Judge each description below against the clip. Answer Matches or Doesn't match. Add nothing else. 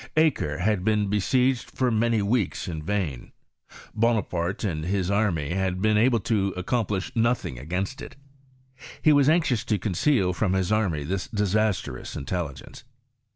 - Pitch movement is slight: Doesn't match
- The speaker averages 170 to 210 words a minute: Doesn't match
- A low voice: Matches